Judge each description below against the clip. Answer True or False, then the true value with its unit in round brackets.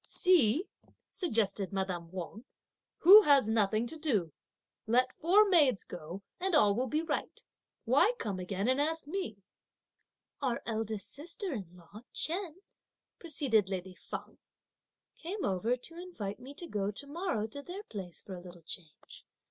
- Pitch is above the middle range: True (235 Hz)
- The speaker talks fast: False (150 wpm)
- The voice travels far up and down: True (8.7 semitones)